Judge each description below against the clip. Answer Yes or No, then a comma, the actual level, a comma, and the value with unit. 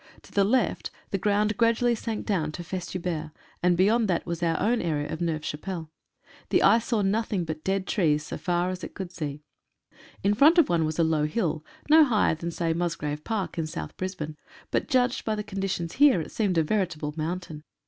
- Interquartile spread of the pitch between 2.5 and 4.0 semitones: No, average, 4.7 semitones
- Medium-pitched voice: Yes, medium, 180 Hz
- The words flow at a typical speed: No, fast, 210 wpm